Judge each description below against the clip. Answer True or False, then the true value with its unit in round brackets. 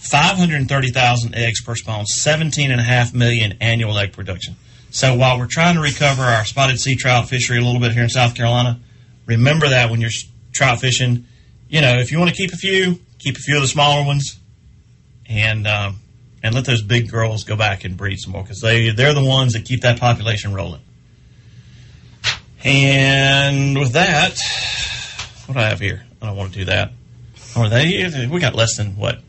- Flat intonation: False (3.1 semitones)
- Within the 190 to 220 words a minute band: True (205 wpm)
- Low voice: True (120 Hz)